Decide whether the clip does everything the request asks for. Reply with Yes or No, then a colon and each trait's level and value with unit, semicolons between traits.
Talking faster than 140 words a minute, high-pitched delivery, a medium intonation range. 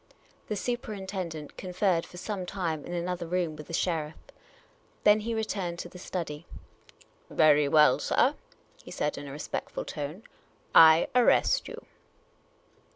No: average, 160 wpm; medium, 175 Hz; average, 4.1 semitones